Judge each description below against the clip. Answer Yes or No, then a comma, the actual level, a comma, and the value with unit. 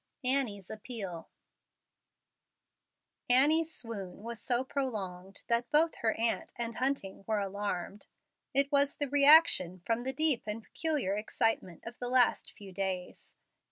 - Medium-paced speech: No, slow, 130 wpm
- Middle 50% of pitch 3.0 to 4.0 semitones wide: No, wide, 5.4 semitones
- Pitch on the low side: No, high, 230 Hz